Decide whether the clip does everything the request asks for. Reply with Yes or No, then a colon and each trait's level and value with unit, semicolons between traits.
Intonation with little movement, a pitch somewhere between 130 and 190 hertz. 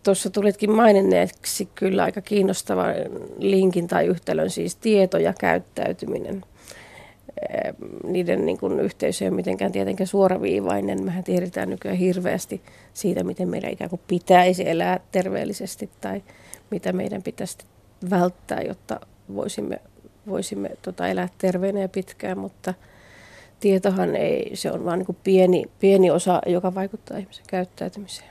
Yes: narrow, 1.9 semitones; medium, 185 Hz